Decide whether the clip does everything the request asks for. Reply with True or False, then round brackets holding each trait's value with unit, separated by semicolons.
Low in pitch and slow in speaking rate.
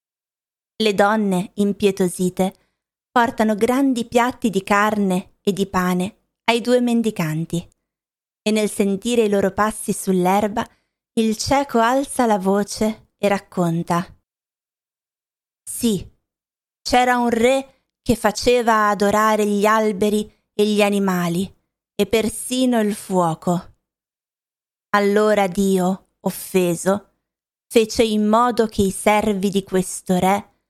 False (210 Hz; 110 wpm)